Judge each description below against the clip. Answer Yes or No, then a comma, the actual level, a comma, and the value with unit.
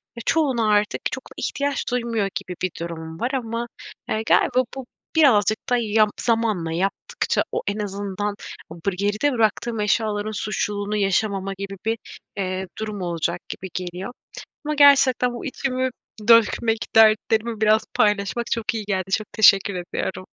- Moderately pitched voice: No, high, 215 Hz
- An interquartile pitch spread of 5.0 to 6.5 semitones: No, average, 3.1 semitones